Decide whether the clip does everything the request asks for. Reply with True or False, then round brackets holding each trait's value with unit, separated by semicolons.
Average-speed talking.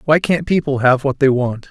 False (245 wpm)